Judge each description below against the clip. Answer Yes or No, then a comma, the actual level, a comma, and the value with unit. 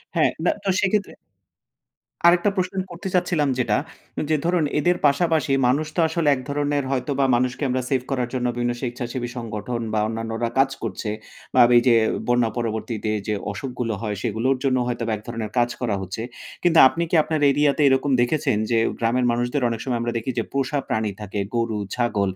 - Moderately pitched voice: No, low, 125 Hz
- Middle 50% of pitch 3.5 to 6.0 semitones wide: Yes, average, 3.9 semitones